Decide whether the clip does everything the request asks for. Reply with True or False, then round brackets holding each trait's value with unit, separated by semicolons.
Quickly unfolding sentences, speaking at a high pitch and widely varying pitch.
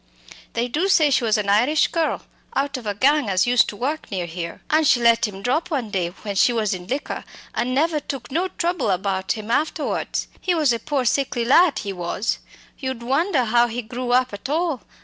True (215 wpm; 245 Hz; 5.8 semitones)